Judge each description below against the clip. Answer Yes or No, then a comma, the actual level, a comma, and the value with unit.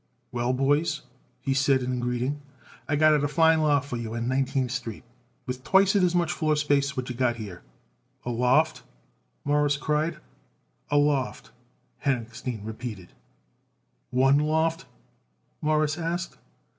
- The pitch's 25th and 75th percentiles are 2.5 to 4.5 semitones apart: Yes, average, 3.6 semitones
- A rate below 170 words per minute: Yes, average, 140 wpm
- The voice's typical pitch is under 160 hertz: Yes, medium, 140 Hz